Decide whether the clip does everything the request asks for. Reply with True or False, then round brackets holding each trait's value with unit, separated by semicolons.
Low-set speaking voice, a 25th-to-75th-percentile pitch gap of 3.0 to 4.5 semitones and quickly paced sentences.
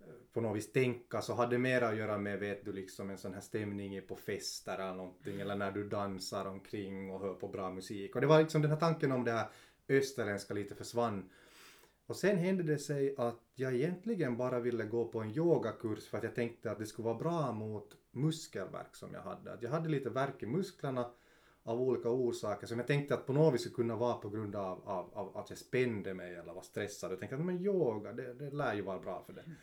False (120 Hz; 5.0 semitones; 235 wpm)